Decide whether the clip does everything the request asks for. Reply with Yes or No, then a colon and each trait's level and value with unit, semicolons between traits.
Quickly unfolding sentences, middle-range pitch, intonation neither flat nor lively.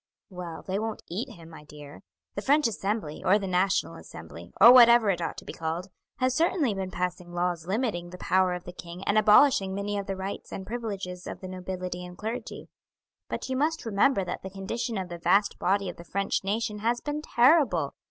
No: fast, 210 wpm; high, 195 Hz; average, 4.0 semitones